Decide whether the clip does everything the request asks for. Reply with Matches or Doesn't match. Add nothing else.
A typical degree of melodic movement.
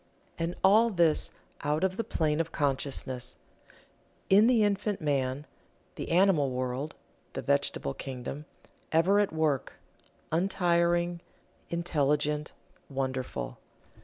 Matches